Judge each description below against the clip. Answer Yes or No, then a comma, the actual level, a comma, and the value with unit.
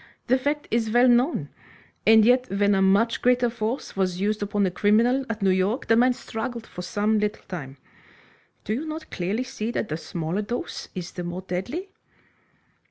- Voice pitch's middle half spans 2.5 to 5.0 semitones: Yes, average, 4.2 semitones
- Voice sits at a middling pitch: No, high, 215 Hz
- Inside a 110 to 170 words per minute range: No, average, 185 wpm